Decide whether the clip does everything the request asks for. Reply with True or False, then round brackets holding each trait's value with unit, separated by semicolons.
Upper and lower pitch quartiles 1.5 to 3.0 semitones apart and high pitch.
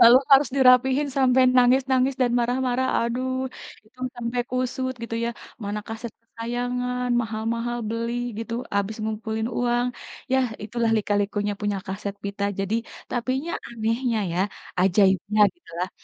True (2.7 semitones; 235 Hz)